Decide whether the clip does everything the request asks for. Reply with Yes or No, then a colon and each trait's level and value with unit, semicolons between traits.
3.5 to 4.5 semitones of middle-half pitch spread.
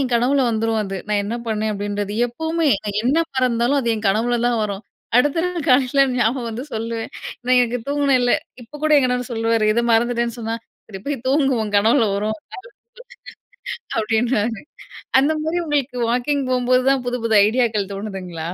No: average, 3.0 semitones